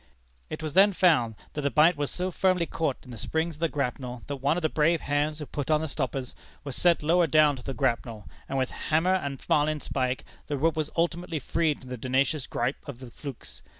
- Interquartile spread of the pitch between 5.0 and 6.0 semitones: No, average, 3.6 semitones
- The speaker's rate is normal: No, fast, 225 wpm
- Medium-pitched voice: Yes, medium, 150 Hz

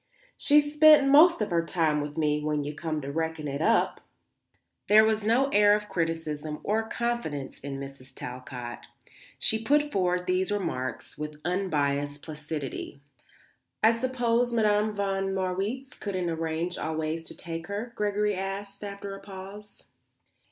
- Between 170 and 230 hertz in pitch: Yes, high, 190 Hz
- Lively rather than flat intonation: Yes, wide, 5.8 semitones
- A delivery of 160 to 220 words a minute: No, average, 145 wpm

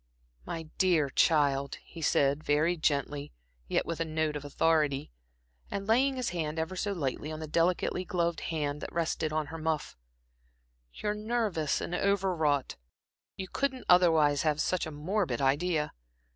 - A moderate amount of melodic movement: Yes, average, 3.5 semitones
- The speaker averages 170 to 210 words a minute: No, average, 160 wpm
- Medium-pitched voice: Yes, medium, 160 Hz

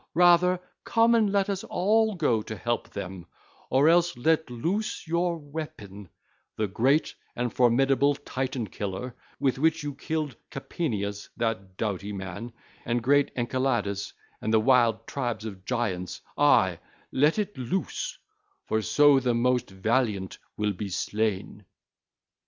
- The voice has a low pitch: Yes, low, 125 Hz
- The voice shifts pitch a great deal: Yes, wide, 6.7 semitones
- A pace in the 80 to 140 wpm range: Yes, slow, 135 wpm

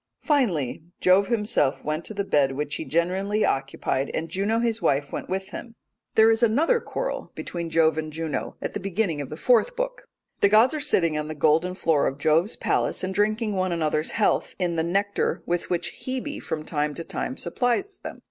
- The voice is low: No, medium, 185 Hz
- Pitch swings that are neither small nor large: No, wide, 6.1 semitones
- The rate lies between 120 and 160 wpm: No, average, 200 wpm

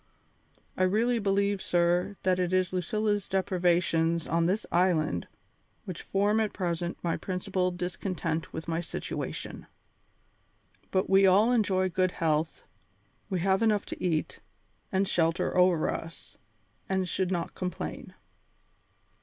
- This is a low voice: No, medium, 185 Hz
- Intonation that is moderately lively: No, narrow, 2.3 semitones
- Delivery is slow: Yes, slow, 130 wpm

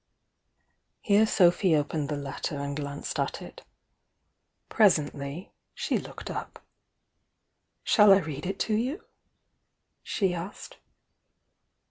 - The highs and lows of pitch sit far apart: Yes, wide, 5.7 semitones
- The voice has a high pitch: No, medium, 170 Hz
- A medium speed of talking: No, slow, 105 wpm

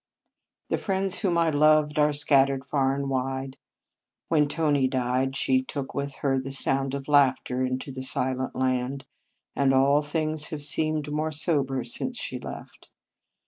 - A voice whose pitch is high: No, medium, 140 Hz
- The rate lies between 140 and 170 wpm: Yes, average, 165 wpm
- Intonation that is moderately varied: No, narrow, 2.2 semitones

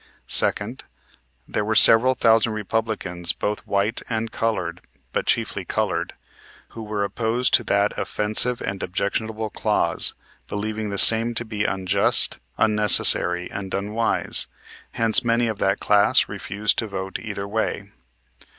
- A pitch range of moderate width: No, narrow, 2.1 semitones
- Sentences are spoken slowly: Yes, slow, 130 wpm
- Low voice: Yes, low, 105 Hz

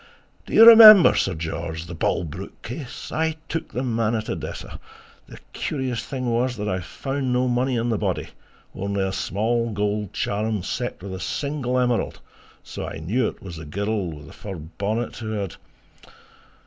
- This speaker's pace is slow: No, average, 185 wpm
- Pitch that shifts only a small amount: No, average, 4.9 semitones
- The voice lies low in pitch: Yes, low, 110 Hz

